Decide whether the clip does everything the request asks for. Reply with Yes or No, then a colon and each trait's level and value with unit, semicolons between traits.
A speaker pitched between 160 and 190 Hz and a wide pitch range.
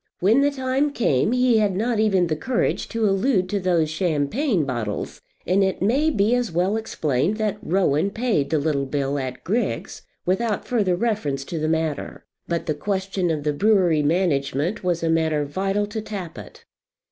Yes: medium, 185 Hz; wide, 5.7 semitones